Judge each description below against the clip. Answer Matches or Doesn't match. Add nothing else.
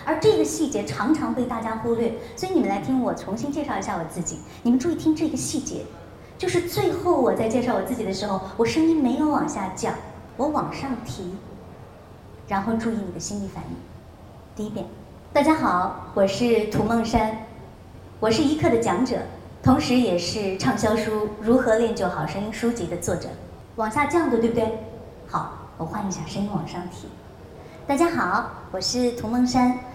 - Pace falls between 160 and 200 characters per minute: Doesn't match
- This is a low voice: Doesn't match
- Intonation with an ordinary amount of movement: Doesn't match